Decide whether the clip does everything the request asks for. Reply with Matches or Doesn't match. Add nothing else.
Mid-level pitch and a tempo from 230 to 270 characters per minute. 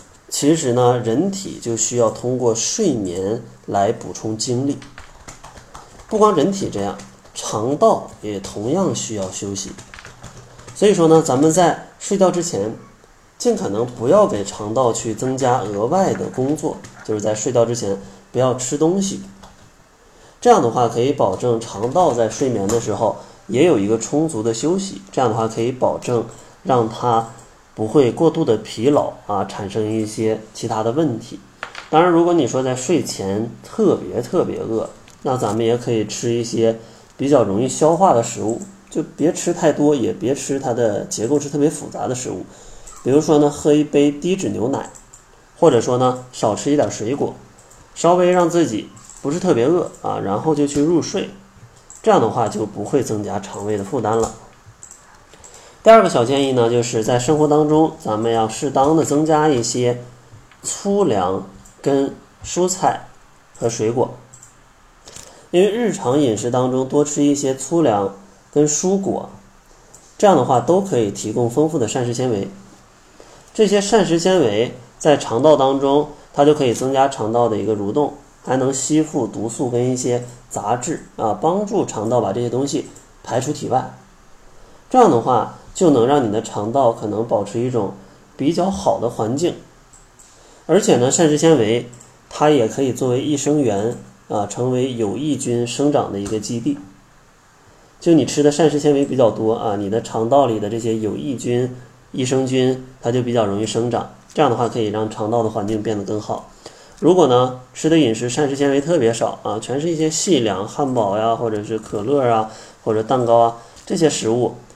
Doesn't match